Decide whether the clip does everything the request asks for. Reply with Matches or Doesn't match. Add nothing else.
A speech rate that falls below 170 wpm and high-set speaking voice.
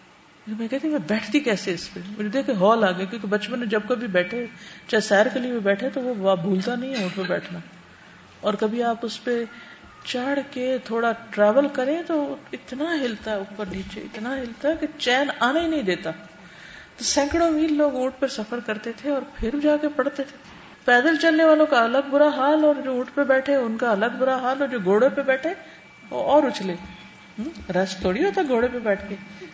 Matches